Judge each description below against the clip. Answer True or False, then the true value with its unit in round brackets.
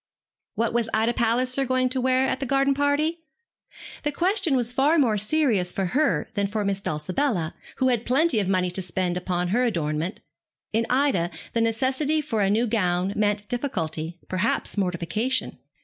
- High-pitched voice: True (230 Hz)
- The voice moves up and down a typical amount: False (6.1 semitones)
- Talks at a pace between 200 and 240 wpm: False (170 wpm)